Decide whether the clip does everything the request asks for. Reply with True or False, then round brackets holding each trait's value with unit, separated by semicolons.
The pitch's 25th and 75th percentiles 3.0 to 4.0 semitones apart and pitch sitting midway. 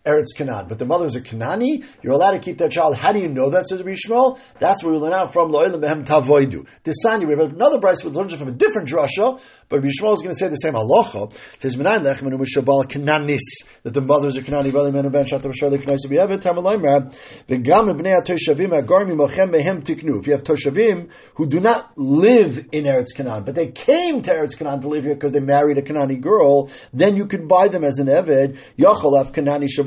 False (5.1 semitones; 150 Hz)